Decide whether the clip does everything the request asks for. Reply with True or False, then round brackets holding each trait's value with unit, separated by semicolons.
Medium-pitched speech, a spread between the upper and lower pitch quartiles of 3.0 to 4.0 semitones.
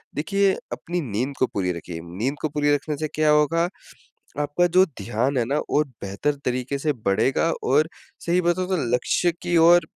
False (145 Hz; 5.1 semitones)